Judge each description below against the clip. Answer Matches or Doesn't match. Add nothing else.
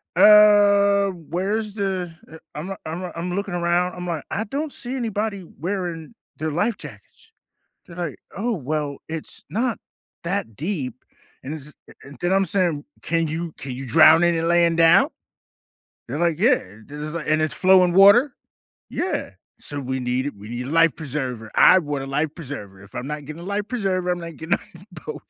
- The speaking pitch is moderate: Matches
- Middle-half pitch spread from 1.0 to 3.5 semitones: Doesn't match